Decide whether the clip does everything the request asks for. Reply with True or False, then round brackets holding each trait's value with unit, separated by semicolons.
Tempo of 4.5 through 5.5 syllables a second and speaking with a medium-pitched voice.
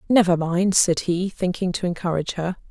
True (5.4 syllables/s; 180 Hz)